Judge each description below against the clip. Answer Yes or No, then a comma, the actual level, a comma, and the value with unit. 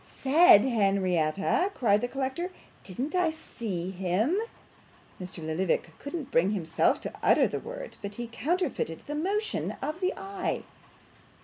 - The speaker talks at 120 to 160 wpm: Yes, average, 140 wpm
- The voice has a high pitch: Yes, high, 245 Hz